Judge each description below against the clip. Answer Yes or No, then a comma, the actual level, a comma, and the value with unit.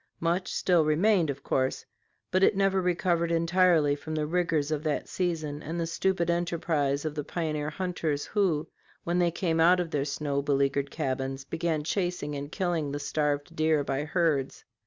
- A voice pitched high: No, medium, 160 Hz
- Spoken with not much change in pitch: No, average, 3.1 semitones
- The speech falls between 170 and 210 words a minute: Yes, average, 175 wpm